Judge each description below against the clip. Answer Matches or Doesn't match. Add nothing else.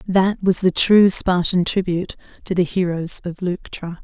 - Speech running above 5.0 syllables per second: Doesn't match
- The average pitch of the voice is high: Doesn't match